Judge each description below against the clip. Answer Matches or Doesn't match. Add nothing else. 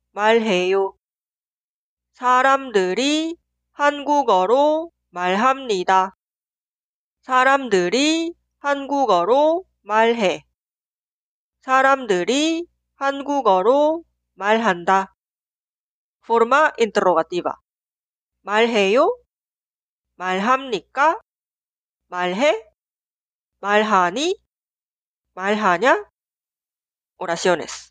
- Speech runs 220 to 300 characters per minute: Doesn't match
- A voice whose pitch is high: Matches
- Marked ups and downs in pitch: Matches